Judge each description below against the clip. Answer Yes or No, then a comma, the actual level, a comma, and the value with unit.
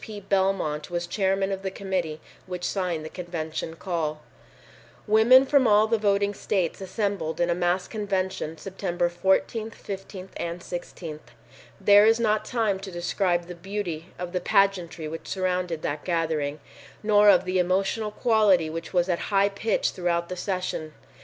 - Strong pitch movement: No, average, 2.8 semitones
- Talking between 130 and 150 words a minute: No, average, 160 wpm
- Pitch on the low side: No, medium, 185 Hz